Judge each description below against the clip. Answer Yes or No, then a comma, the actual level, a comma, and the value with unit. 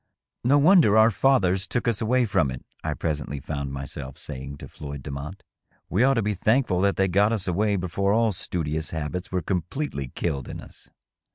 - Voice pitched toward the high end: No, very low, 95 Hz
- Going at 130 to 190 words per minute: No, average, 200 wpm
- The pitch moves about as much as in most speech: No, wide, 6.8 semitones